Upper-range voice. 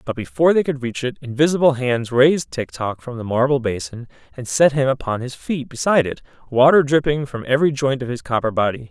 No: low, 130 Hz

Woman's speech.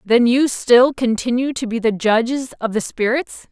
Yes: female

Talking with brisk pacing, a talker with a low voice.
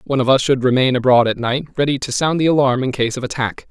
Yes: fast, 275 wpm; low, 130 Hz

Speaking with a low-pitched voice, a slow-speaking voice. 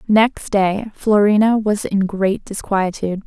No: high, 205 Hz; slow, 130 wpm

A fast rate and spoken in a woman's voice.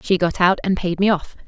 Yes: fast, 285 wpm; female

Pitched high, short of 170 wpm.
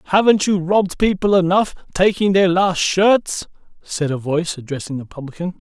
No: medium, 180 Hz; average, 150 wpm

